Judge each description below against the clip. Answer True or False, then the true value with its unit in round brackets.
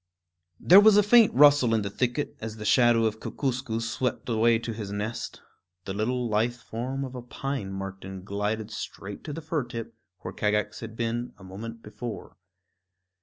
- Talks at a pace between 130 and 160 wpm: False (175 wpm)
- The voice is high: False (115 Hz)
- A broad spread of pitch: False (3.1 semitones)